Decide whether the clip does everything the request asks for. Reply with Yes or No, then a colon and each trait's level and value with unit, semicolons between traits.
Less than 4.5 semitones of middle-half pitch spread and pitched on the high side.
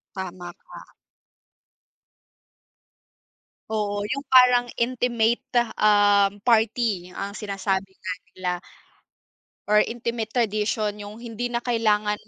Yes: narrow, 2.6 semitones; high, 210 Hz